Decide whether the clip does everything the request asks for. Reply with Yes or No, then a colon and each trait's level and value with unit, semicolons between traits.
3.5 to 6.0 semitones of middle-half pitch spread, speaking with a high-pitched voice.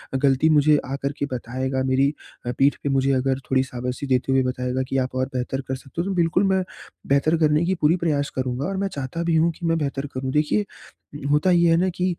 No: average, 4.0 semitones; medium, 140 Hz